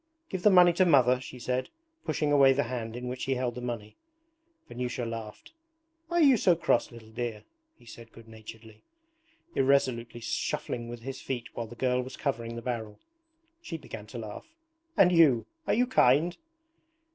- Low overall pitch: Yes, low, 125 Hz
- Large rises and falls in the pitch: No, average, 3.3 semitones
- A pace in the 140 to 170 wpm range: No, average, 180 wpm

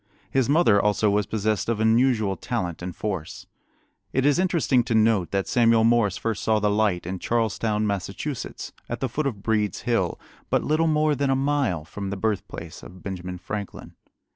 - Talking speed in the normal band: Yes, average, 180 wpm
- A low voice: Yes, low, 110 Hz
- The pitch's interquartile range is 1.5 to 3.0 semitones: No, average, 3.8 semitones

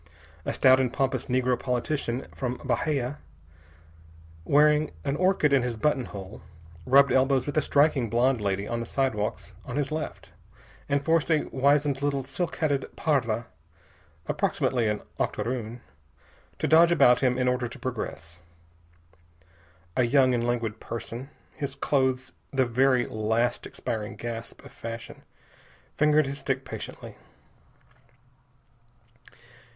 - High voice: No, low, 130 Hz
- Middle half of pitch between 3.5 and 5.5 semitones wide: No, average, 3.1 semitones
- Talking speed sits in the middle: No, slow, 130 wpm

